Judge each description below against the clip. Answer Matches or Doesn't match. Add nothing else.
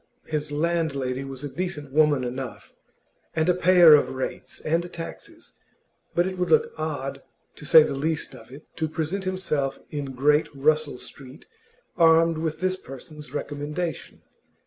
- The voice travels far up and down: Doesn't match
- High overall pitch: Doesn't match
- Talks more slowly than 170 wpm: Matches